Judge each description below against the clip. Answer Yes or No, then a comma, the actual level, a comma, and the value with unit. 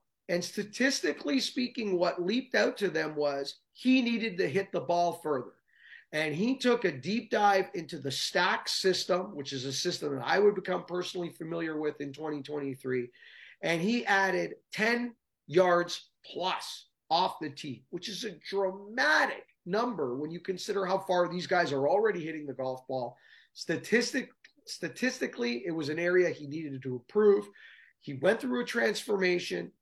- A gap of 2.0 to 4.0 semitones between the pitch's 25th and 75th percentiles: No, wide, 5.4 semitones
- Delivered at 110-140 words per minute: No, average, 165 wpm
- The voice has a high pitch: No, medium, 180 Hz